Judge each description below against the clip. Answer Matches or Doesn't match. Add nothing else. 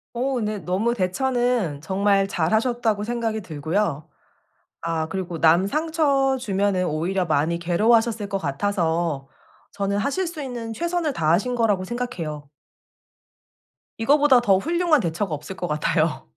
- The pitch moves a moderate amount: Doesn't match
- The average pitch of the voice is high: Matches